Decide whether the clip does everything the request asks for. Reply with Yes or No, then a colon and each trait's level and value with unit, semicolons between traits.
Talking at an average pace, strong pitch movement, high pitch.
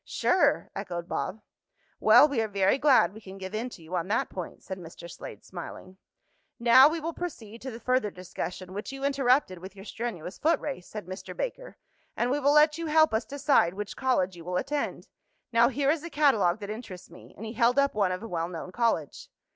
No: fast, 220 wpm; wide, 6.9 semitones; high, 220 Hz